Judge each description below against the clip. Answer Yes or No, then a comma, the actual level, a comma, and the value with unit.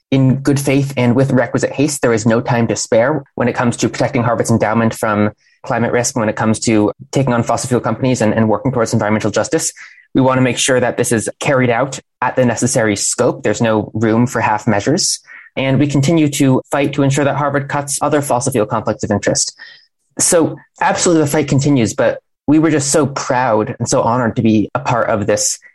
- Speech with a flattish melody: No, average, 4.0 semitones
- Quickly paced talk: Yes, fast, 220 wpm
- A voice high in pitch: No, low, 125 Hz